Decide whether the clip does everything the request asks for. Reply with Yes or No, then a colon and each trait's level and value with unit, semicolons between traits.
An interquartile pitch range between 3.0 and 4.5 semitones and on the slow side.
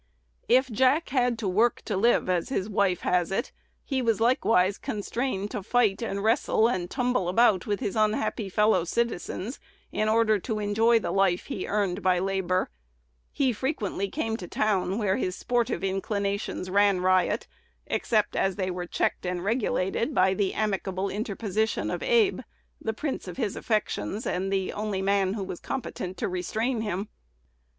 No: average, 3.4 semitones; average, 165 wpm